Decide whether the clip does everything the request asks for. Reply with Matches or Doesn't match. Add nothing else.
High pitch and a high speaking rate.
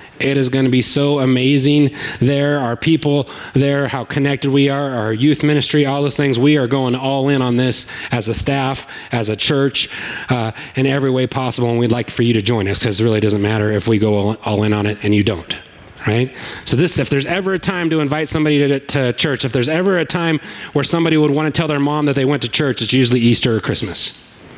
Doesn't match